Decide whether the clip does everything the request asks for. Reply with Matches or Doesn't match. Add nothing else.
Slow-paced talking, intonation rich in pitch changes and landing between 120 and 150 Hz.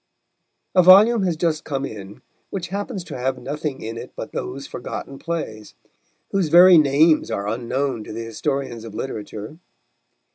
Doesn't match